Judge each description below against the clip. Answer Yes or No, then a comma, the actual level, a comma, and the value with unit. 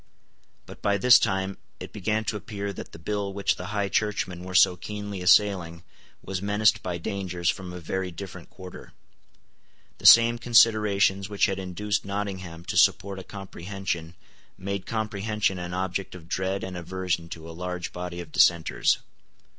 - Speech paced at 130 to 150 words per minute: No, average, 160 wpm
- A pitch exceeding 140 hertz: No, very low, 95 Hz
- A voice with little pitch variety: Yes, narrow, 2.3 semitones